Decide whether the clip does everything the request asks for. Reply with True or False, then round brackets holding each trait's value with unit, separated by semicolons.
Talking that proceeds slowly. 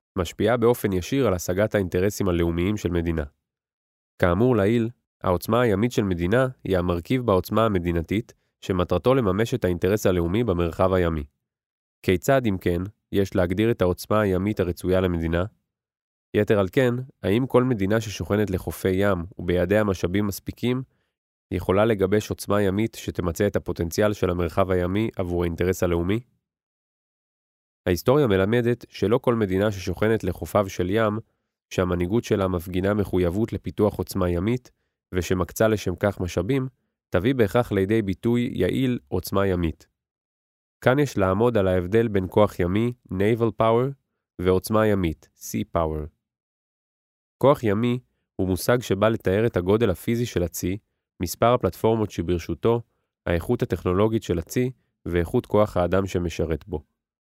False (130 wpm)